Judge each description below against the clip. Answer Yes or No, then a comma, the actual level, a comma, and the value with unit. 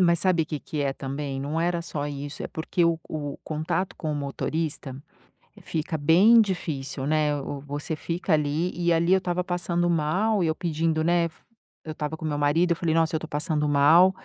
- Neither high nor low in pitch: Yes, medium, 160 Hz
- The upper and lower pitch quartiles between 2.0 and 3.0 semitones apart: Yes, average, 2.7 semitones